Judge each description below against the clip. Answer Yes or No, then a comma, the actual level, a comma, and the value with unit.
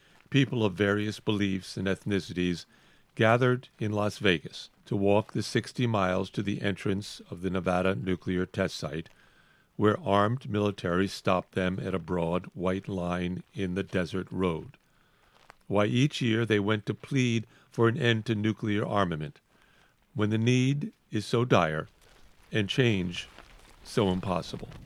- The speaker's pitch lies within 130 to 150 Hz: No, low, 100 Hz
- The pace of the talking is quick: No, average, 145 wpm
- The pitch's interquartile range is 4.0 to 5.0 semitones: No, average, 3.3 semitones